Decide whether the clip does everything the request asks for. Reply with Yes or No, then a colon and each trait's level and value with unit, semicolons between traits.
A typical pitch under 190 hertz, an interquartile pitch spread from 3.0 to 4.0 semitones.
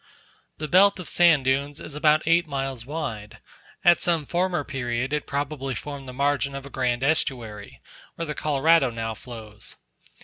Yes: medium, 140 Hz; average, 3.5 semitones